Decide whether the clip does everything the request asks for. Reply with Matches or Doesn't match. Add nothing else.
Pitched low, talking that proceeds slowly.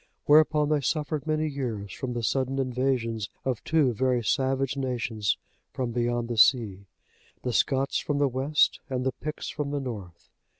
Doesn't match